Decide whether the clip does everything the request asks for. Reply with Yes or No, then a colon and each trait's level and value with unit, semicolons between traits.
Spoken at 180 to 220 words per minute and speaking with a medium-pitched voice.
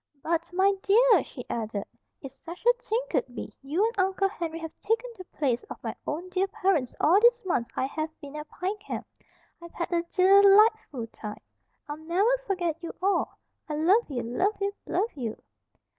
No: average, 190 wpm; very high, 355 Hz